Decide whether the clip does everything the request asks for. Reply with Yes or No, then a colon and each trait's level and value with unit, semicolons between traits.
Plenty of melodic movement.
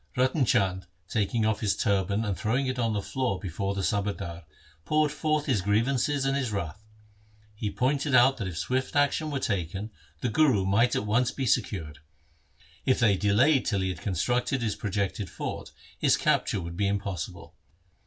No: average, 4.8 semitones